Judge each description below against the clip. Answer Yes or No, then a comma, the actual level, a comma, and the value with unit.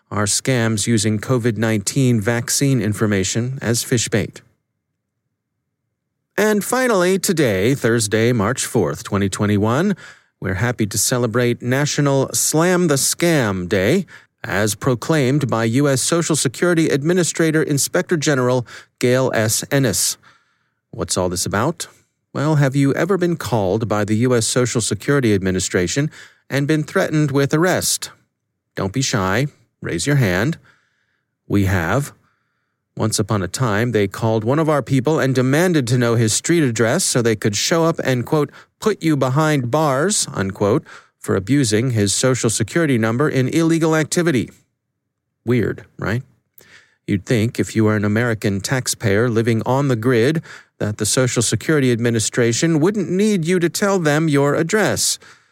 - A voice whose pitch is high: No, low, 130 Hz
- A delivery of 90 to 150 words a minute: Yes, average, 140 wpm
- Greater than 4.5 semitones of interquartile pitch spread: Yes, wide, 5.5 semitones